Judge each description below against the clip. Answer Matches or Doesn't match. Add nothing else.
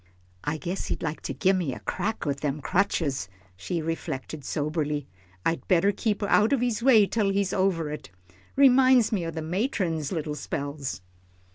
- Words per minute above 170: Doesn't match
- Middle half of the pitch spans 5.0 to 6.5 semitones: Matches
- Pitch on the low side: Doesn't match